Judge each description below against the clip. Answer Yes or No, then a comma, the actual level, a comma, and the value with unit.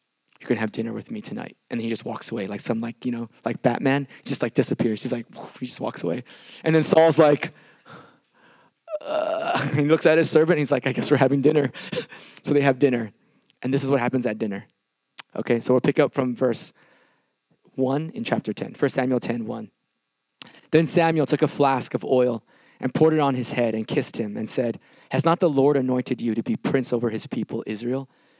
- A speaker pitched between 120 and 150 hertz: Yes, low, 135 Hz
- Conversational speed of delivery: No, fast, 220 wpm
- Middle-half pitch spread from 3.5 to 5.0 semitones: Yes, average, 4.1 semitones